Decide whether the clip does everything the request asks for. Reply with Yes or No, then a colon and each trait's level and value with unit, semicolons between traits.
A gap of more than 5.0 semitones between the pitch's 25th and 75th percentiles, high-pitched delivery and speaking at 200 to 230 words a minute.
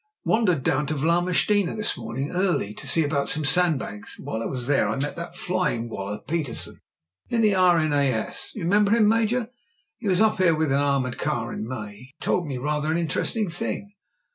No: wide, 5.6 semitones; medium, 155 Hz; fast, 205 wpm